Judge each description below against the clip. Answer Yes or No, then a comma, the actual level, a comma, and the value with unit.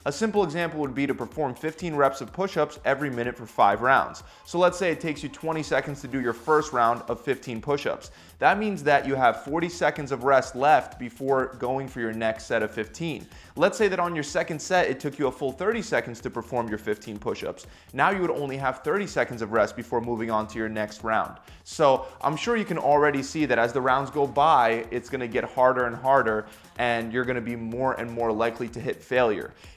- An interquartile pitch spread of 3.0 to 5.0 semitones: Yes, average, 4.3 semitones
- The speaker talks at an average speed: No, fast, 235 wpm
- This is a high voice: No, low, 135 Hz